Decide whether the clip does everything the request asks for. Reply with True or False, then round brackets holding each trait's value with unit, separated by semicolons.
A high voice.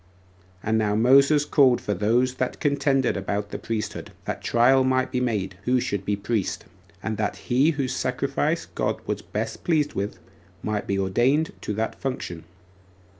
False (120 Hz)